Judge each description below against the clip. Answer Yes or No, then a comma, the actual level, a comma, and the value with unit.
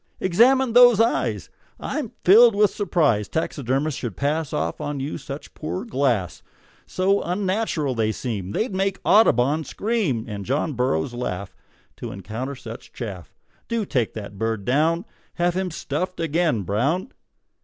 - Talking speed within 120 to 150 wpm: Yes, average, 145 wpm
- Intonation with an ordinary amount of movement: No, wide, 8.2 semitones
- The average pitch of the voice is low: No, medium, 150 Hz